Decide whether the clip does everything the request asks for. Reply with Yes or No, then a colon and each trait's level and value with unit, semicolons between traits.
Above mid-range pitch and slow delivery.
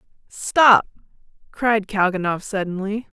Yes: high, 205 Hz; slow, 75 wpm